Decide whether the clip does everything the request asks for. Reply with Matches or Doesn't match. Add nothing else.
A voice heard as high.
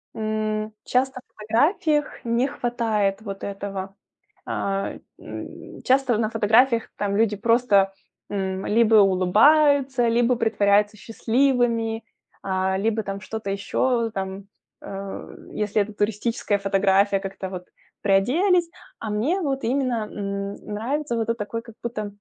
Matches